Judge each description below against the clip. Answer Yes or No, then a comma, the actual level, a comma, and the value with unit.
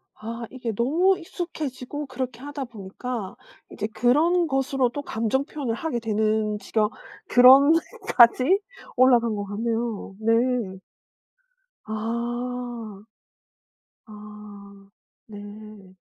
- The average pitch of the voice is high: Yes, high, 235 Hz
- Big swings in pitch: No, average, 3.5 semitones